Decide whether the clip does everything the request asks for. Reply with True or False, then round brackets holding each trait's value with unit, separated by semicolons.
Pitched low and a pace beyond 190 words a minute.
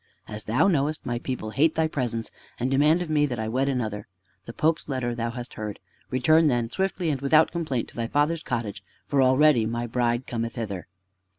True (125 Hz; 200 wpm)